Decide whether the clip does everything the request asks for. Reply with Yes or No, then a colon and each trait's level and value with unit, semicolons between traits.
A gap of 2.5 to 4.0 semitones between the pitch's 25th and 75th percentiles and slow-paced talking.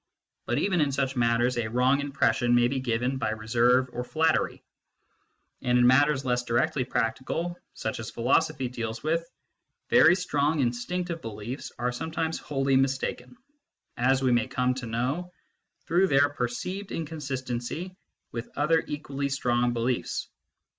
No: average, 3.7 semitones; average, 145 wpm